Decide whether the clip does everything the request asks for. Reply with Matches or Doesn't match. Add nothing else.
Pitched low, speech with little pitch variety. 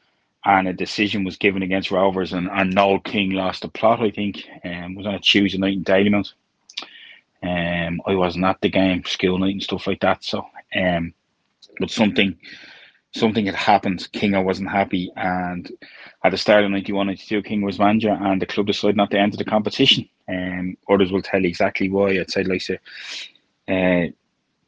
Matches